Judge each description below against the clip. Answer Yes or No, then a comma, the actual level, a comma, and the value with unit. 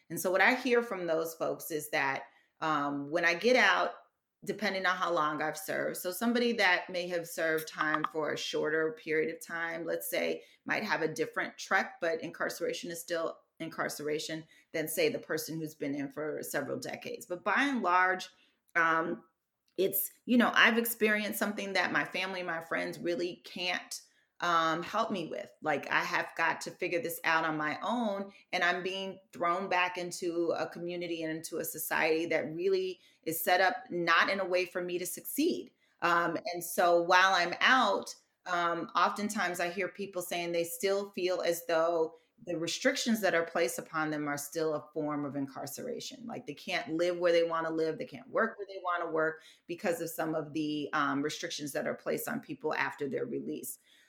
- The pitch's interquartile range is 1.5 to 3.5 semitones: Yes, average, 2.7 semitones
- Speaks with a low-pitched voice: No, medium, 170 Hz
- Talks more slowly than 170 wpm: No, average, 195 wpm